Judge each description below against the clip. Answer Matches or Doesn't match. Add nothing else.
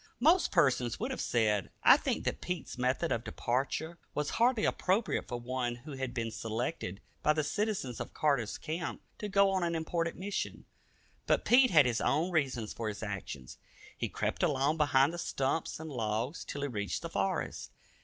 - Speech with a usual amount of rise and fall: Doesn't match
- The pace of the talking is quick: Doesn't match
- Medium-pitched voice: Matches